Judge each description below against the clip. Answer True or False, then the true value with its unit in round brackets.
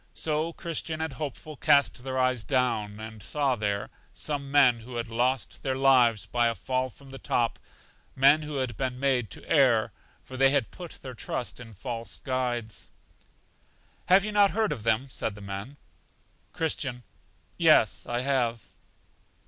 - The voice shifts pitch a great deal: False (3.3 semitones)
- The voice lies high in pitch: False (130 Hz)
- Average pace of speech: True (165 wpm)